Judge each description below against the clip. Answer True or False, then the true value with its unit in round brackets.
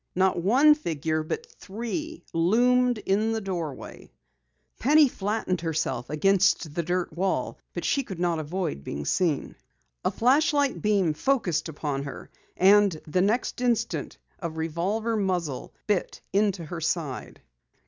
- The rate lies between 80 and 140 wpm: True (135 wpm)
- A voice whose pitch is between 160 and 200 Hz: True (190 Hz)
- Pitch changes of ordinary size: False (5.7 semitones)